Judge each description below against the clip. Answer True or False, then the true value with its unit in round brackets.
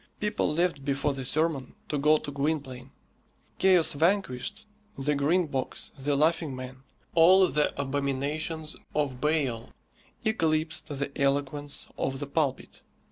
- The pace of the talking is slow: True (130 wpm)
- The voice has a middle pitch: True (145 Hz)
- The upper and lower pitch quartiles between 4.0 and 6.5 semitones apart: False (2.7 semitones)